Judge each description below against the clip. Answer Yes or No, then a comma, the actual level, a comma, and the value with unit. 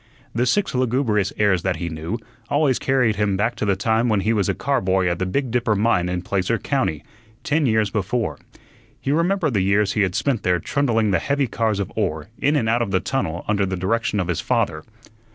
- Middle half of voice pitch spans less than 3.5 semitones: No, average, 4.7 semitones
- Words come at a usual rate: No, fast, 225 wpm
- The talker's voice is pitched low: Yes, low, 105 Hz